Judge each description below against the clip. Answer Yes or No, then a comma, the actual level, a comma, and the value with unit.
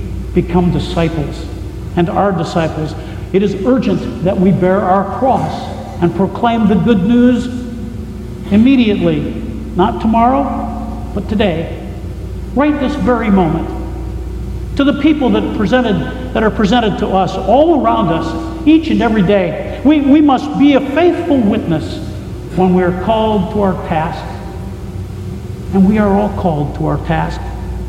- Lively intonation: Yes, wide, 8.4 semitones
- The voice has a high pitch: Yes, high, 195 Hz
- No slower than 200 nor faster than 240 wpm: No, average, 140 wpm